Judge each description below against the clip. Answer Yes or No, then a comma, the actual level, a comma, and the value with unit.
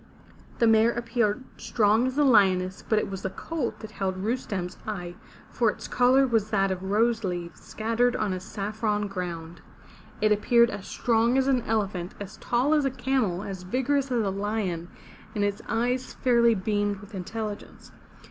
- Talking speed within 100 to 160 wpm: No, average, 175 wpm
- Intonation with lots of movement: No, average, 3.6 semitones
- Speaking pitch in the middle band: No, high, 215 Hz